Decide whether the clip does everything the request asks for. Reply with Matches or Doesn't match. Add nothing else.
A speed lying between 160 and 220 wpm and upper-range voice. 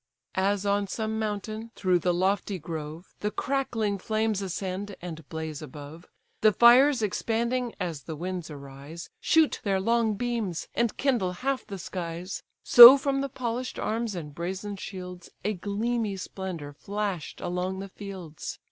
Doesn't match